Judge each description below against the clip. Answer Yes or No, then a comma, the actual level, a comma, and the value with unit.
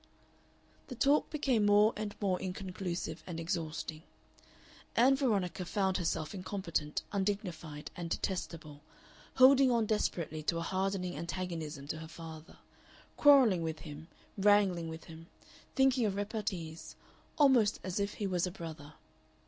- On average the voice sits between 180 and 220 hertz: Yes, medium, 185 Hz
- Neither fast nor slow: No, slow, 130 wpm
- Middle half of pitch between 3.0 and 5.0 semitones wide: Yes, average, 4.3 semitones